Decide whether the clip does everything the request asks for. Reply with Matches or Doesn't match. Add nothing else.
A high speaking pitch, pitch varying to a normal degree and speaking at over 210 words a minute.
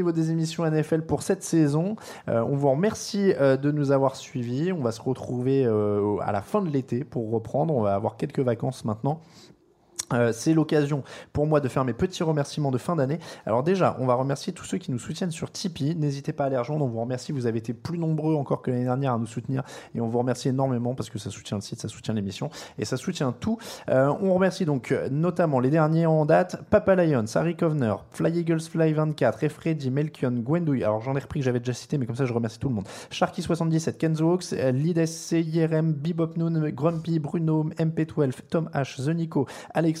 Doesn't match